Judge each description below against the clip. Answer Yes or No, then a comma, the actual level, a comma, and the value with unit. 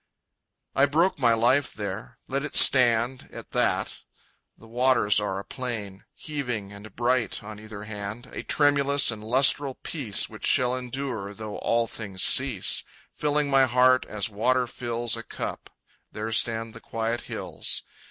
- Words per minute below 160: Yes, average, 150 wpm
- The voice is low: Yes, low, 120 Hz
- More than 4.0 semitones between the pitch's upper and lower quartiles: No, average, 3.5 semitones